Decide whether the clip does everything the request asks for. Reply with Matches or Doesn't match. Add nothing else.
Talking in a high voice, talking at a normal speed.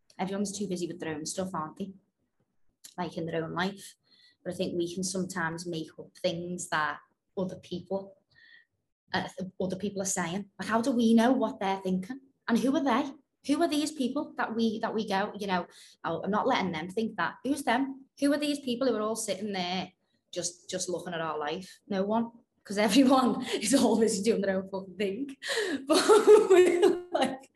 Matches